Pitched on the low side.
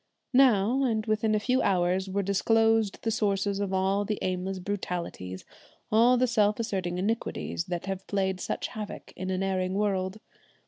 No: high, 200 Hz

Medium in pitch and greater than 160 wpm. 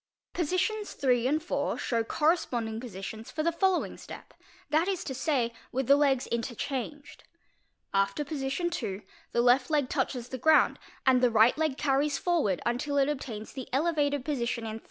No: very high, 270 Hz; average, 170 wpm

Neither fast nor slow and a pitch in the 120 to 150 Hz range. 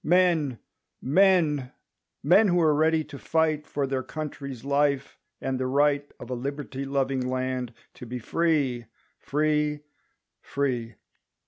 No: slow, 120 wpm; medium, 140 Hz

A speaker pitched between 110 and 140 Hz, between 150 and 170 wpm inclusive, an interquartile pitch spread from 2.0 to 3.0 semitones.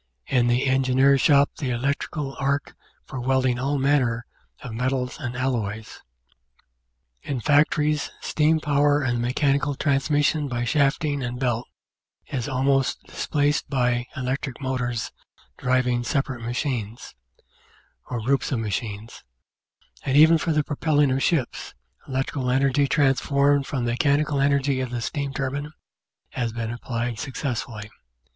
No: low, 135 Hz; slow, 135 wpm; average, 2.7 semitones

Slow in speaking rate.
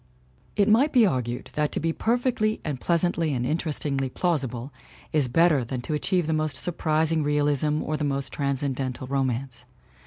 No: average, 175 wpm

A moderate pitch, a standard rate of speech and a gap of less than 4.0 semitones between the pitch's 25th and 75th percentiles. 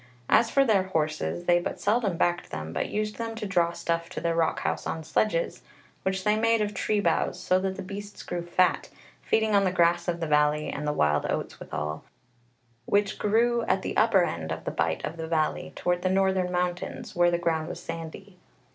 No: medium, 180 Hz; fast, 210 wpm; average, 3.5 semitones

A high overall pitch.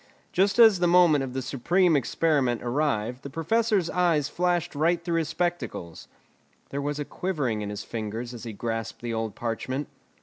No: medium, 145 Hz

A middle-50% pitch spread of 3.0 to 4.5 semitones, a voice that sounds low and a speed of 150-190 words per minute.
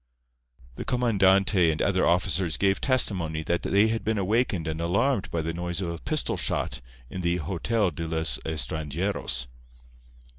Yes: average, 3.7 semitones; very low, 90 Hz; average, 155 wpm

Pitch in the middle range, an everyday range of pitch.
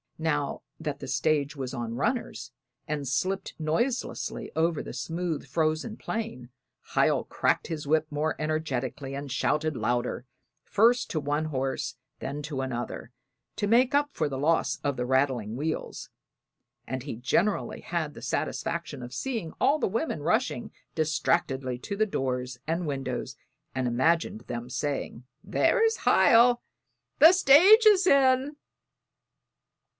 No: medium, 155 Hz; wide, 7.6 semitones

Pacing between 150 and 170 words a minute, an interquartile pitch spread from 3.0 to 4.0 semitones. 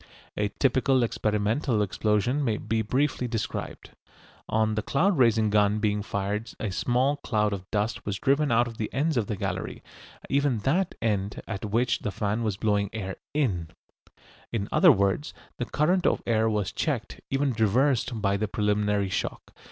Yes: average, 165 wpm; average, 3.6 semitones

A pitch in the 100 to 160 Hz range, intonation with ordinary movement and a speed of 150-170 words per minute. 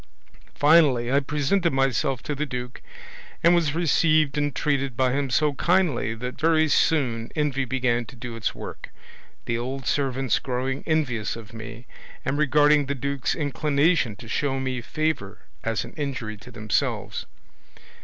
Yes: low, 135 Hz; average, 3.6 semitones; average, 155 wpm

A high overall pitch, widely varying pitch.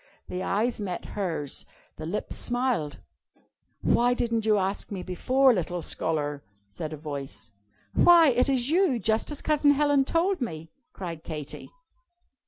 Yes: high, 210 Hz; wide, 8.5 semitones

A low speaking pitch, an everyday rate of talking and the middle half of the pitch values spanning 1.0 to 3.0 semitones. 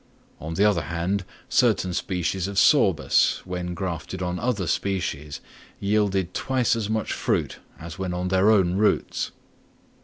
Yes: very low, 95 Hz; average, 145 wpm; narrow, 2.4 semitones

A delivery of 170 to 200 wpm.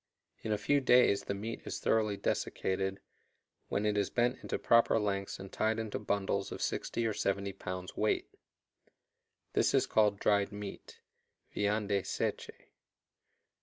No: average, 145 wpm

